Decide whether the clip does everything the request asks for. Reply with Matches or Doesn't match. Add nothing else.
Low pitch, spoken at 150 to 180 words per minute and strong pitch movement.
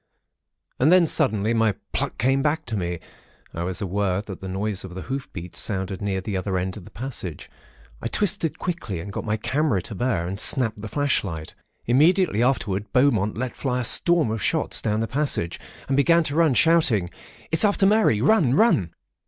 Doesn't match